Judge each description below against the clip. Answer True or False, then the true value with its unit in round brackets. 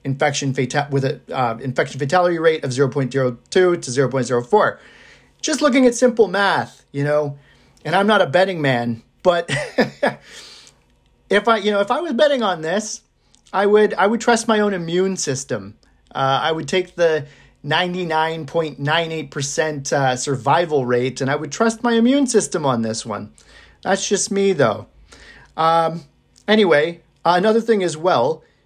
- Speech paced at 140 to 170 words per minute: False (180 wpm)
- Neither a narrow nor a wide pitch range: False (6.4 semitones)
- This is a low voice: False (160 Hz)